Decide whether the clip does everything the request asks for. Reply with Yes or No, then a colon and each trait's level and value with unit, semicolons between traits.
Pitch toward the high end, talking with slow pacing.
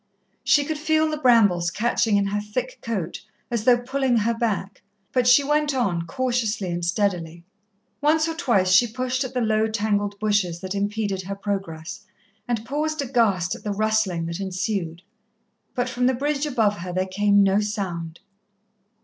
No: high, 215 Hz; average, 170 wpm